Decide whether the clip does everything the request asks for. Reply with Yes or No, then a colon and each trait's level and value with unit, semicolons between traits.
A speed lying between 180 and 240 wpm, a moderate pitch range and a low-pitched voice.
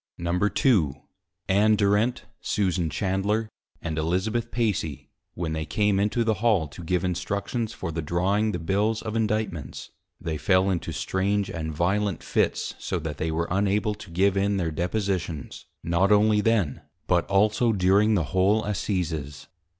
No: average, 150 wpm; average, 3.6 semitones; very low, 95 Hz